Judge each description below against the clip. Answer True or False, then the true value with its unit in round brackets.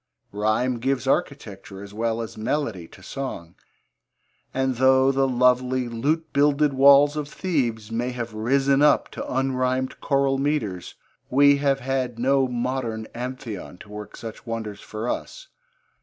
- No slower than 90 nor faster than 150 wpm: True (140 wpm)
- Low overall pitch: True (130 Hz)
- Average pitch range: True (3.3 semitones)